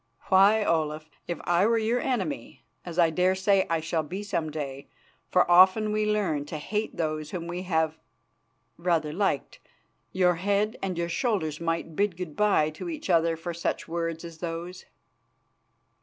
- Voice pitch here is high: No, medium, 170 Hz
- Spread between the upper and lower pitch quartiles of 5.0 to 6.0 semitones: No, average, 3.5 semitones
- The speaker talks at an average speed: Yes, average, 170 wpm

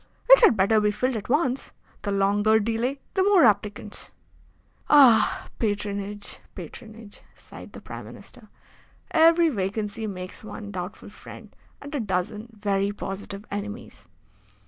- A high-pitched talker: Yes, high, 210 Hz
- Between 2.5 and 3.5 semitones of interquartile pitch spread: Yes, average, 2.9 semitones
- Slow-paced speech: Yes, slow, 130 wpm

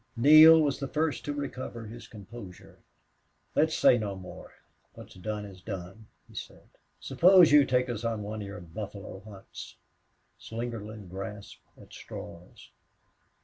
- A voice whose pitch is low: Yes, low, 110 Hz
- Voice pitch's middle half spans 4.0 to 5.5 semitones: Yes, average, 5.2 semitones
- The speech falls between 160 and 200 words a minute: No, average, 145 wpm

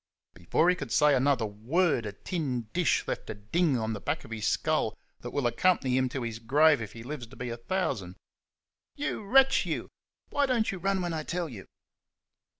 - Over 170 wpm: Yes, fast, 205 wpm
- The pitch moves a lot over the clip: Yes, wide, 7.4 semitones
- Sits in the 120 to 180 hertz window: Yes, medium, 140 Hz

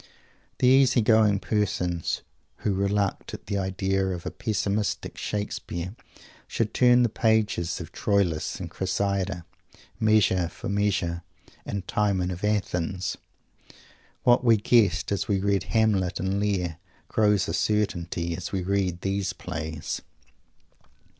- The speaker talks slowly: Yes, slow, 125 wpm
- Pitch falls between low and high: No, low, 100 Hz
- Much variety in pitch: No, average, 2.8 semitones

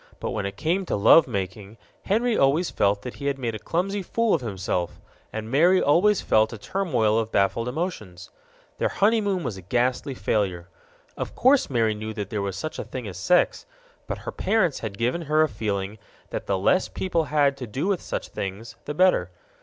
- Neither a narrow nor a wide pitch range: No, wide, 8.9 semitones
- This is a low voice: Yes, low, 125 Hz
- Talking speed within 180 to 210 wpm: Yes, average, 200 wpm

